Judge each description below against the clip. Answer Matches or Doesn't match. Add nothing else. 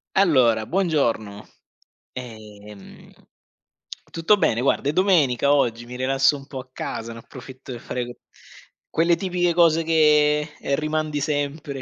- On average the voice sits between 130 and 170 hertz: Matches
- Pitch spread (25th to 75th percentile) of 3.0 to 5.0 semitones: Matches